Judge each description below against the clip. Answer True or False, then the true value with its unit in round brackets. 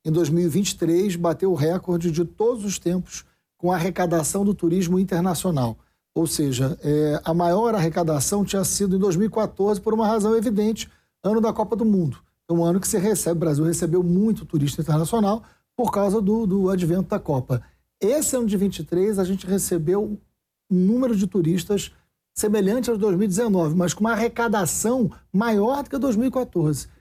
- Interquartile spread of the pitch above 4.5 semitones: False (4.0 semitones)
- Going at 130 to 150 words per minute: False (165 wpm)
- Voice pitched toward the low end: False (190 Hz)